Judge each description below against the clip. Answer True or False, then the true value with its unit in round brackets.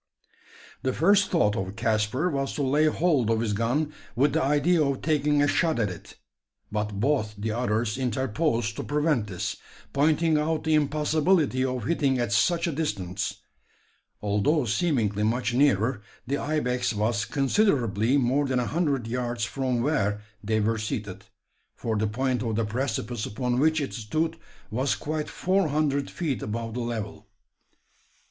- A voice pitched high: False (130 Hz)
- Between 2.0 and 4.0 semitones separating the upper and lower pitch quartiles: False (5.2 semitones)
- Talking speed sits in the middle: True (160 wpm)